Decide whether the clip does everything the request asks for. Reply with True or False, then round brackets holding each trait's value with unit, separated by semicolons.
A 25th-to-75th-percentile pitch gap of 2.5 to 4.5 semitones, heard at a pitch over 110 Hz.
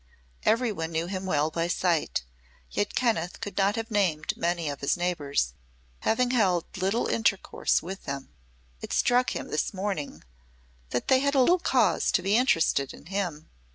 False (5.6 semitones; 185 Hz)